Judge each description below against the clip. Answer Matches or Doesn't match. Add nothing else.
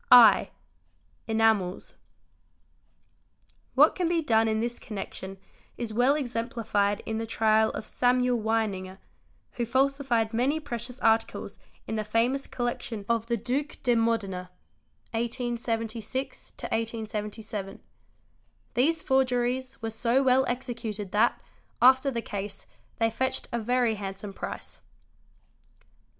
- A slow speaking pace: Matches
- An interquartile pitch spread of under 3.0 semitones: Matches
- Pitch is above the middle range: Matches